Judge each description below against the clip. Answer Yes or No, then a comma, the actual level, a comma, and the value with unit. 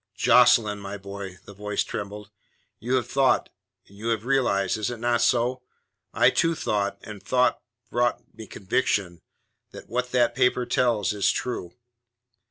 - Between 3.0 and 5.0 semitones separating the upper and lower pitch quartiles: Yes, average, 3.6 semitones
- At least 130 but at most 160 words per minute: Yes, average, 155 wpm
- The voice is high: No, low, 110 Hz